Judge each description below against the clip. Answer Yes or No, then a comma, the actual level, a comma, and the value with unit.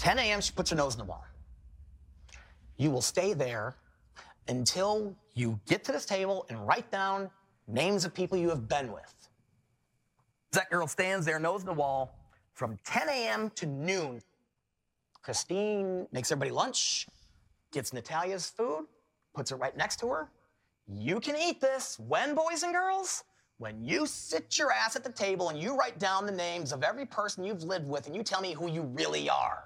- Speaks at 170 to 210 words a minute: Yes, average, 185 wpm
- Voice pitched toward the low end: No, medium, 175 Hz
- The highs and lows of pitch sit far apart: Yes, wide, 8.1 semitones